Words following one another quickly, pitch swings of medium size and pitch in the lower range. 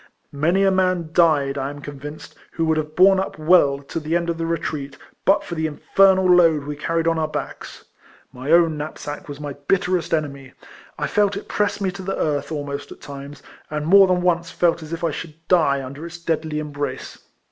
No: fast, 210 wpm; average, 3.4 semitones; medium, 160 Hz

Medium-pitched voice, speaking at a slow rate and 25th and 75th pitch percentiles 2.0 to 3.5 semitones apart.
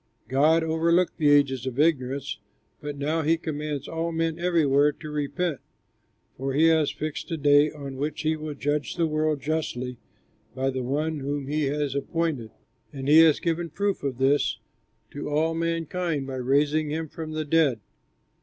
No: medium, 150 Hz; average, 170 wpm; narrow, 2.6 semitones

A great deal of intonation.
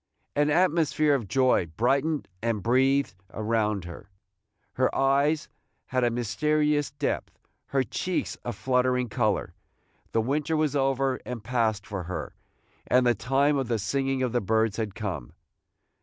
No: average, 4.1 semitones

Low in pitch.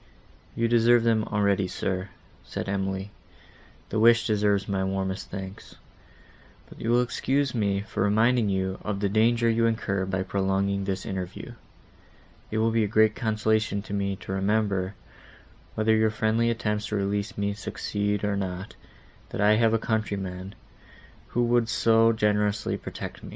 Yes: low, 105 Hz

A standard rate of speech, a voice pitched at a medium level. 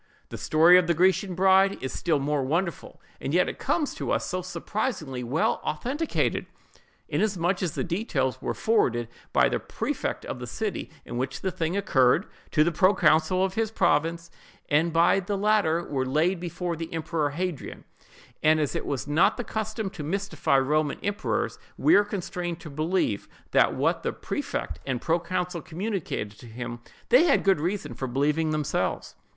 Yes: average, 170 wpm; medium, 170 Hz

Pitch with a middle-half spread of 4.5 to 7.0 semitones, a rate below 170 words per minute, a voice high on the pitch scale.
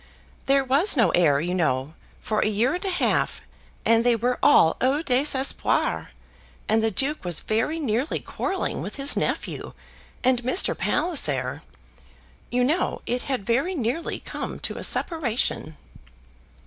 Yes: average, 5.1 semitones; average, 150 wpm; very high, 250 Hz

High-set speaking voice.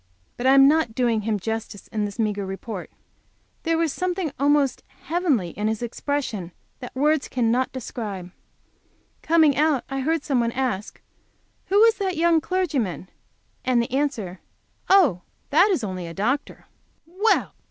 Yes: very high, 260 Hz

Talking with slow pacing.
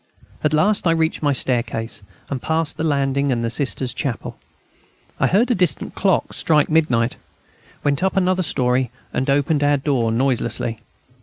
No: average, 160 wpm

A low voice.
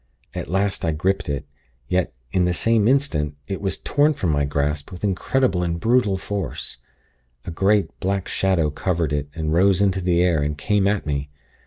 Yes: very low, 90 Hz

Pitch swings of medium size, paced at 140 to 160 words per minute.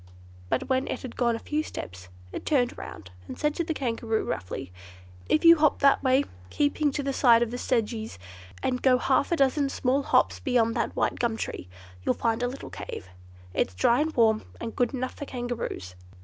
No: average, 3.4 semitones; fast, 205 wpm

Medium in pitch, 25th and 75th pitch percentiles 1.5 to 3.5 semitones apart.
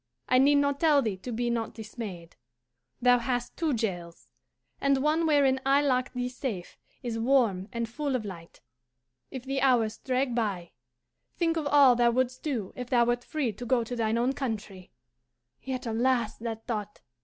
No: high, 245 Hz; average, 3.2 semitones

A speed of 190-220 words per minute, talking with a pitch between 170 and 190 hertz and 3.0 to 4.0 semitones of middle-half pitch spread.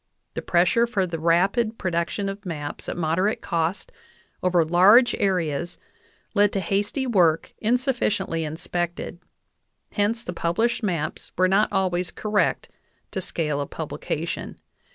No: slow, 135 wpm; medium, 185 Hz; average, 3.5 semitones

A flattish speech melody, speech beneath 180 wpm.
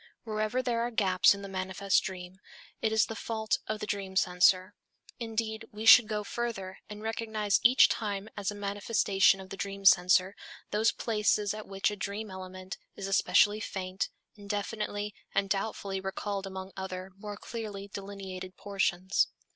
Yes: narrow, 2.0 semitones; average, 160 wpm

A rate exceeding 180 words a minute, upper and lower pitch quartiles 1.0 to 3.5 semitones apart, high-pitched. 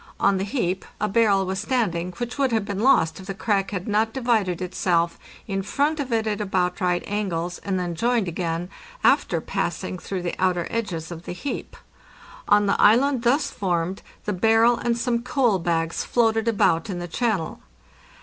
No: average, 190 wpm; average, 4.5 semitones; high, 195 Hz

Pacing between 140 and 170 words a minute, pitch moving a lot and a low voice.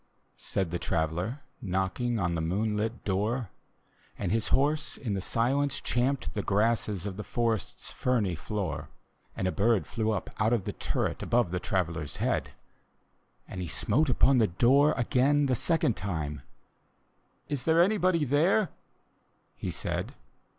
Yes: average, 155 wpm; wide, 6.0 semitones; low, 110 Hz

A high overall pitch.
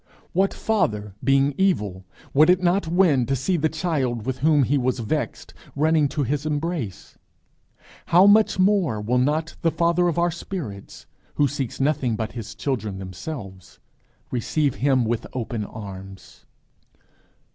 No: low, 135 Hz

